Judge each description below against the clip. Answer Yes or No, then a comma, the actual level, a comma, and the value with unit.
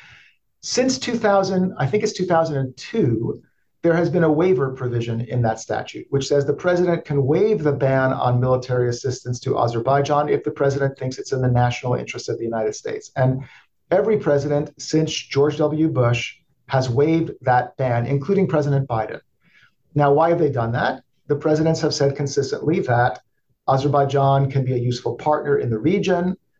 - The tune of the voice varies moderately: Yes, average, 3.9 semitones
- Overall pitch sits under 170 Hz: Yes, medium, 140 Hz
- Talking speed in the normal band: Yes, average, 170 wpm